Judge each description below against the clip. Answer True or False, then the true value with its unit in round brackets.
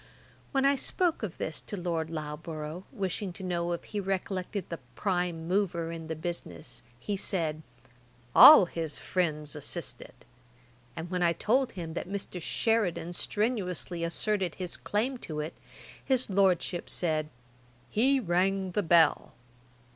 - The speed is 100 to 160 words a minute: True (140 wpm)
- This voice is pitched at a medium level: True (180 Hz)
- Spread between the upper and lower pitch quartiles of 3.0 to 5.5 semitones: True (3.5 semitones)